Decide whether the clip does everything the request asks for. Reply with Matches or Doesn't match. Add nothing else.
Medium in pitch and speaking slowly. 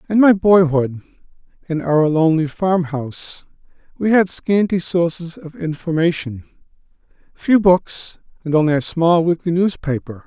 Matches